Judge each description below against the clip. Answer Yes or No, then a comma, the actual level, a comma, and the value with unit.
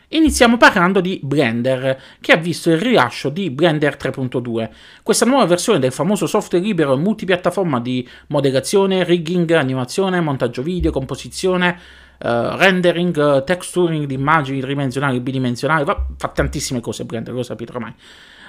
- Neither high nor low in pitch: Yes, medium, 150 Hz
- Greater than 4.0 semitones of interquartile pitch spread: Yes, wide, 5.5 semitones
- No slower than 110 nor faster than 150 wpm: Yes, average, 145 wpm